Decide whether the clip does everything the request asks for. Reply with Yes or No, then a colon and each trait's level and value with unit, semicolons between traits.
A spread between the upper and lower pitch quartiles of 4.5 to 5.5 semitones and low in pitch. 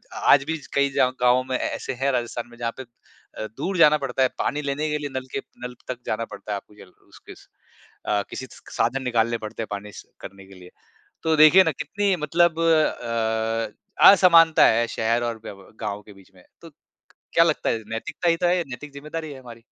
Yes: average, 5.0 semitones; low, 130 Hz